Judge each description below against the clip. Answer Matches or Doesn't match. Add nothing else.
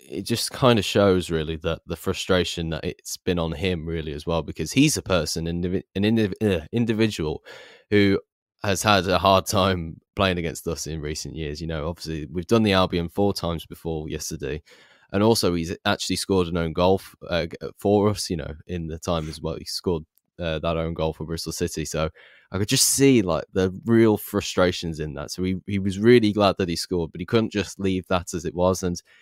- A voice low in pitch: Matches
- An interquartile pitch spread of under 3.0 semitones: Doesn't match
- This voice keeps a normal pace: Doesn't match